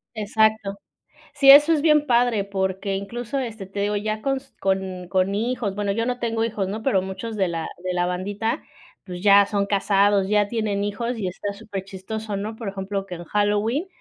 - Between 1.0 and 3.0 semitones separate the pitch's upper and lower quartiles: Yes, average, 2.7 semitones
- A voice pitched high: Yes, high, 205 Hz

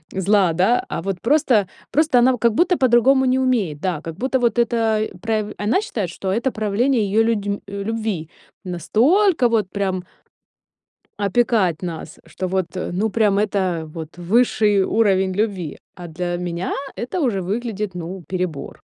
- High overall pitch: Yes, high, 205 Hz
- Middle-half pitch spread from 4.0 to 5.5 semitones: Yes, average, 4.5 semitones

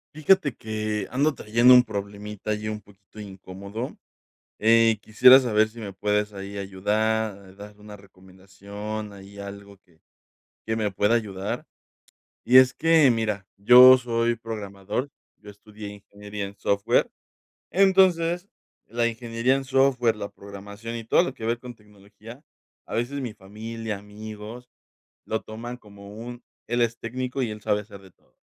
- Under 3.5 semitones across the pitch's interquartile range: Yes, average, 2.7 semitones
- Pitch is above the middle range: No, low, 110 Hz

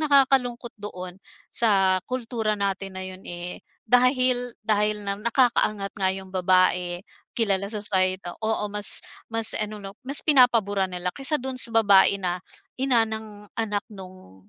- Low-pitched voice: No, high, 205 Hz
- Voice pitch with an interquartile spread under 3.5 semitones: No, average, 3.9 semitones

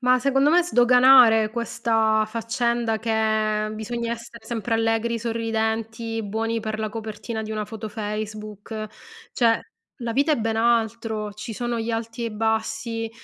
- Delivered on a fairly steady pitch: Yes, narrow, 1.3 semitones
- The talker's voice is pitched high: Yes, high, 225 Hz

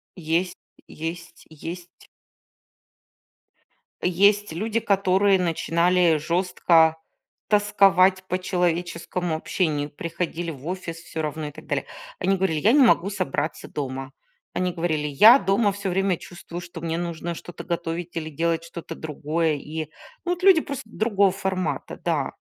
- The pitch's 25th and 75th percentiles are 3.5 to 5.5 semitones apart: No, average, 2.9 semitones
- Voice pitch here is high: No, medium, 175 Hz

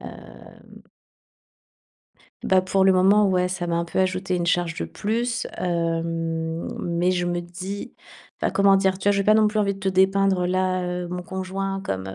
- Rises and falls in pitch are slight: Yes, narrow, 1.9 semitones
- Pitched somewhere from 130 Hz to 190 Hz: Yes, medium, 185 Hz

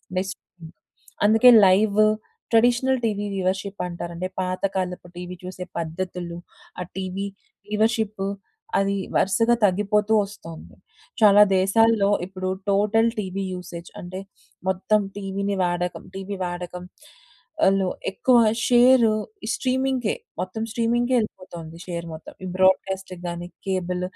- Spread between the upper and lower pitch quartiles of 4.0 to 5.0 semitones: No, average, 2.9 semitones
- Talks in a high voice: Yes, high, 195 Hz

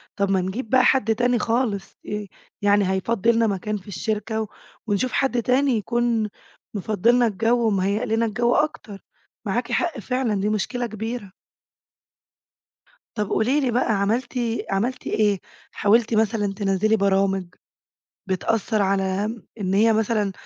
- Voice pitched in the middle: No, high, 215 Hz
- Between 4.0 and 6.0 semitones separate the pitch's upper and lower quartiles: No, average, 3.0 semitones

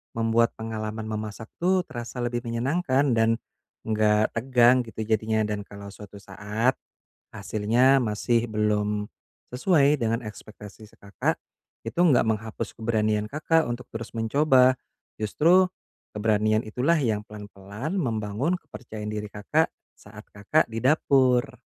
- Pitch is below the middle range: Yes, low, 110 Hz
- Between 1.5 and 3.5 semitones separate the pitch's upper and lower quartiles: Yes, average, 3.1 semitones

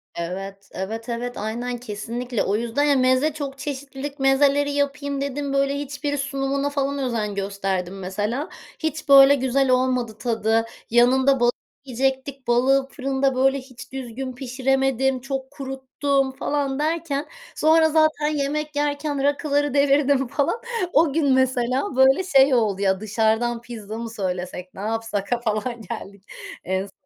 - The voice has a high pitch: Yes, very high, 265 Hz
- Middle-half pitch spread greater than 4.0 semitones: No, average, 3.4 semitones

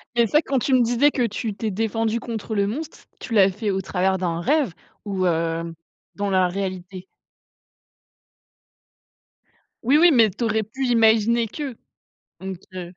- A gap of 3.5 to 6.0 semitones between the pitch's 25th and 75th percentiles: Yes, average, 3.9 semitones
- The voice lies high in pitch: Yes, high, 215 Hz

